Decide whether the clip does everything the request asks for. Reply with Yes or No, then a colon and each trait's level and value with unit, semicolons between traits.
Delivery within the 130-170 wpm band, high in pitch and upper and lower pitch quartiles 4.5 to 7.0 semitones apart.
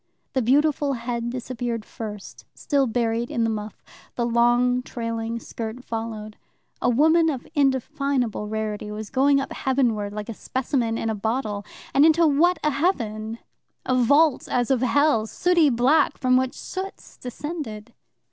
No: average, 155 wpm; high, 245 Hz; average, 3.7 semitones